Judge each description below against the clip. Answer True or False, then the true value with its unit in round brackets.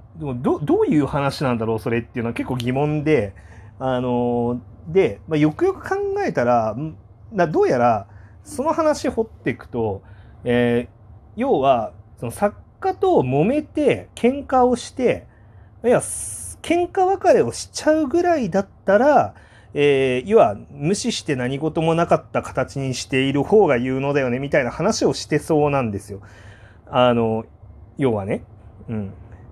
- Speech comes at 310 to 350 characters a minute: False (285 characters per minute)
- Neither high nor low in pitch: False (130 Hz)